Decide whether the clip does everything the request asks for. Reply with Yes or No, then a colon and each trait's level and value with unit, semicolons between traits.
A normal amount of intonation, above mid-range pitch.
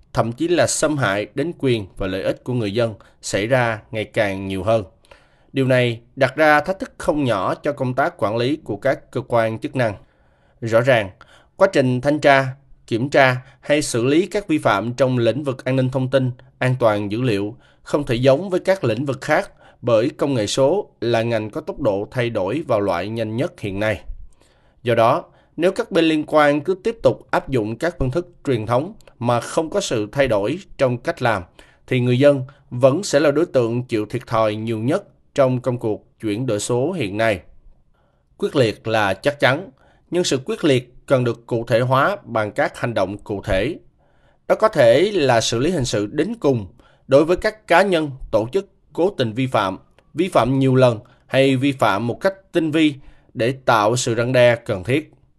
No: average, 4.2 semitones; low, 130 Hz